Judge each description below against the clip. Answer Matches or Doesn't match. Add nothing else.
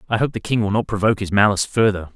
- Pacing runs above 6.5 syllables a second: Matches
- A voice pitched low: Matches